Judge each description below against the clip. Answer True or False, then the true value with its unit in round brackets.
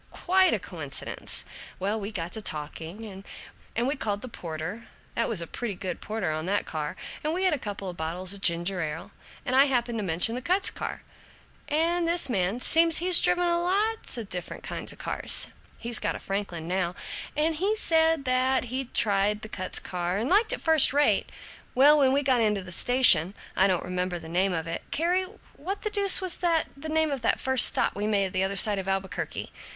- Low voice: False (225 Hz)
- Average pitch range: False (8.7 semitones)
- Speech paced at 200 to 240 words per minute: True (205 wpm)